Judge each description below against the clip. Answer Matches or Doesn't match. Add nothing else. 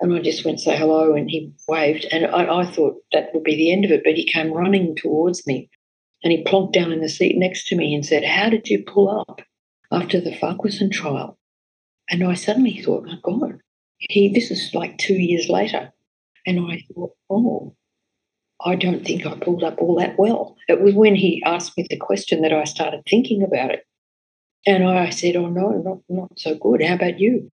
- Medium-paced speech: Doesn't match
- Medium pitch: Matches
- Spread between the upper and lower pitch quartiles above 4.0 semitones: Doesn't match